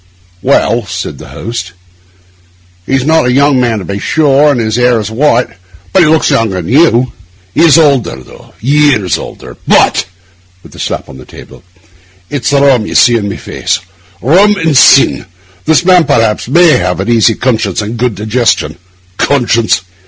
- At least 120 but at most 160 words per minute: No, average, 175 wpm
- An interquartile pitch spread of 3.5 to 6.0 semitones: Yes, average, 5.2 semitones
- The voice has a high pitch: No, low, 120 Hz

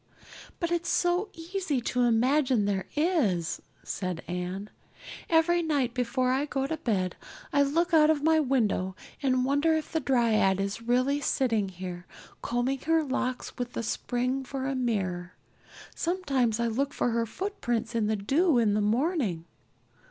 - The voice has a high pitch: Yes, very high, 255 Hz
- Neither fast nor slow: Yes, average, 160 wpm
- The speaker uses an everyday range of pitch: No, wide, 5.7 semitones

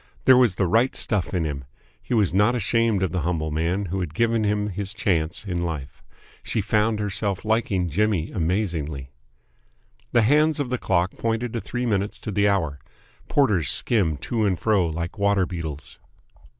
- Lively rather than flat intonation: No, average, 4.6 semitones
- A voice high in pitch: No, low, 100 Hz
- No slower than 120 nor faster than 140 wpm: No, average, 175 wpm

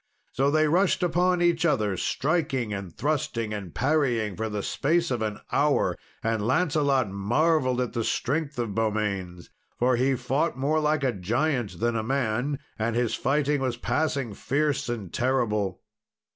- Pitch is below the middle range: Yes, low, 130 Hz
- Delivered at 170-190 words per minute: No, average, 160 wpm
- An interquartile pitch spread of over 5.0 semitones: Yes, wide, 5.4 semitones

